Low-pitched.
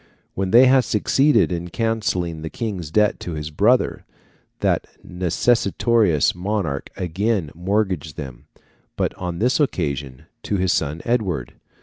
Yes: very low, 95 Hz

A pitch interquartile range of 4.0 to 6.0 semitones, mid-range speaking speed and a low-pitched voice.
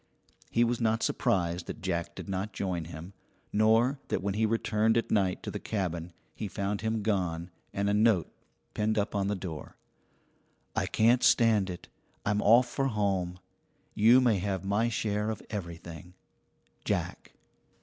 No: average, 3.3 semitones; average, 160 wpm; low, 100 Hz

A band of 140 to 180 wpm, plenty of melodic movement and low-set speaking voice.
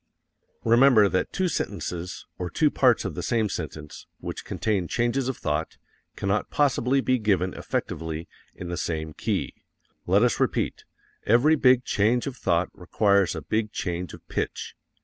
Yes: average, 155 wpm; wide, 5.9 semitones; low, 105 Hz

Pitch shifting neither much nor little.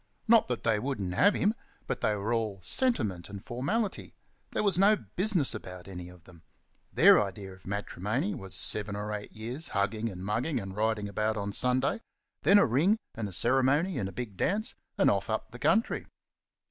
No: wide, 7.0 semitones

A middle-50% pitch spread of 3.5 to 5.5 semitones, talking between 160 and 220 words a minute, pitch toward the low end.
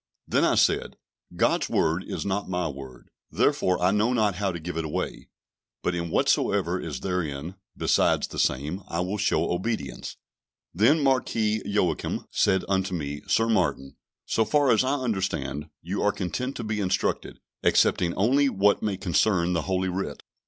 Yes: average, 4.1 semitones; average, 165 wpm; very low, 95 Hz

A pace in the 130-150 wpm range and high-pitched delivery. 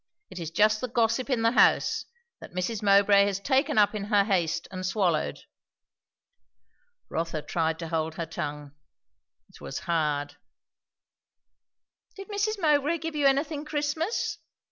Yes: average, 145 wpm; high, 205 Hz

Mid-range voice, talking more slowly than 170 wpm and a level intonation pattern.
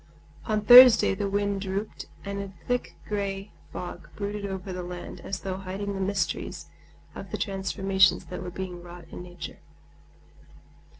No: high, 195 Hz; average, 155 wpm; narrow, 1.6 semitones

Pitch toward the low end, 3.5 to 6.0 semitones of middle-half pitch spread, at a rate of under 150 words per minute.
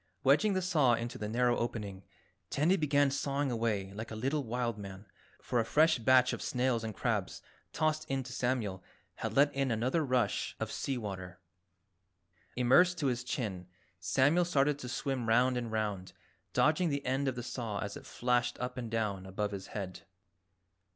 No: low, 125 Hz; average, 4.0 semitones; average, 180 wpm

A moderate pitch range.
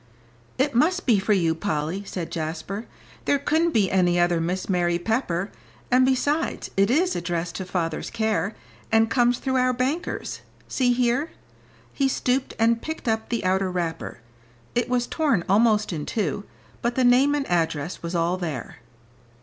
No: wide, 6.4 semitones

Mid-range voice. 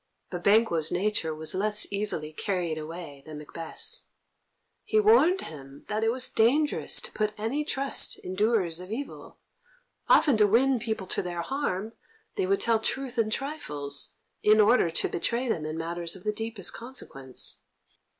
No: high, 210 Hz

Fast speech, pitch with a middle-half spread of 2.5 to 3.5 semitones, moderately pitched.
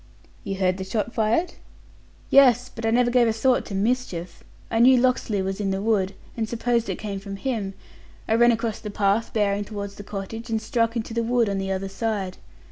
No: fast, 210 wpm; average, 3.1 semitones; high, 220 Hz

